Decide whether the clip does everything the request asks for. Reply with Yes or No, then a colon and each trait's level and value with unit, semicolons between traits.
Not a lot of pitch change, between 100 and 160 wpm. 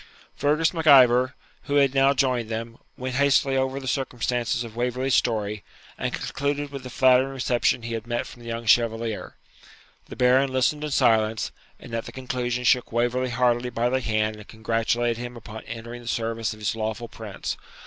No: narrow, 2.3 semitones; average, 185 wpm